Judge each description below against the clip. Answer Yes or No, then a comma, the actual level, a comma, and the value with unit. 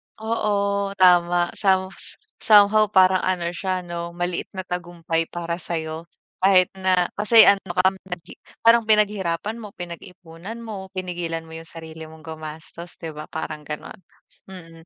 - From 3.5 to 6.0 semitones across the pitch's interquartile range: No, average, 3.0 semitones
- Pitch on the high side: No, medium, 180 Hz